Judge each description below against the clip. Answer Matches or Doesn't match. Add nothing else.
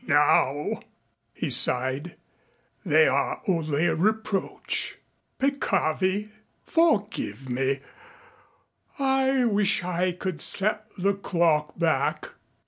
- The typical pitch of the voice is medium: Matches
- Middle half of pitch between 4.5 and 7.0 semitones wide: Matches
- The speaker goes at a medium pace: Doesn't match